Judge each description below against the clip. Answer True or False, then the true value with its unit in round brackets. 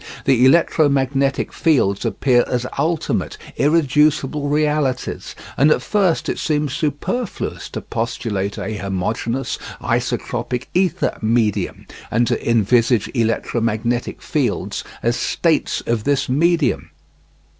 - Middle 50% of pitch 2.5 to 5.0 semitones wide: True (4.4 semitones)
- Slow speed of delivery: True (105 wpm)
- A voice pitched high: False (130 Hz)